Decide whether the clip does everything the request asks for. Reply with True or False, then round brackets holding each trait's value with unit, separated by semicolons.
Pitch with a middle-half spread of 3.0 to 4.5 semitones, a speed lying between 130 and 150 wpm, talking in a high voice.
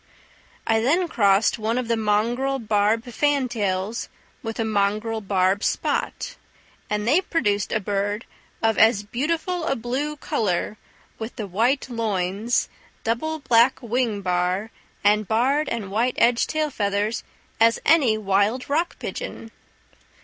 True (3.7 semitones; 135 wpm; 225 Hz)